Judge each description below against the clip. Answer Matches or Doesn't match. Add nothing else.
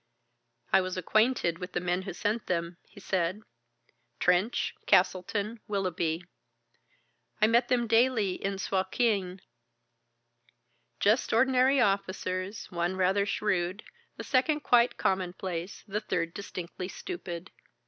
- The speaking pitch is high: Matches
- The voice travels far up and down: Doesn't match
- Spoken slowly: Matches